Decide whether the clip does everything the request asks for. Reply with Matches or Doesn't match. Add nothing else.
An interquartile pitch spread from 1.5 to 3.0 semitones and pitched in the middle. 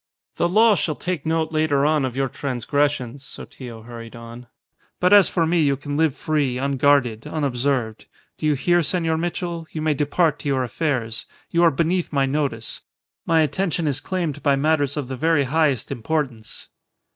Doesn't match